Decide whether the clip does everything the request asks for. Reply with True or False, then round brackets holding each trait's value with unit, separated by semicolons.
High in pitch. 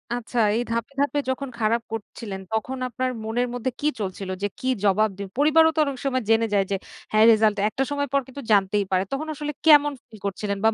True (230 Hz)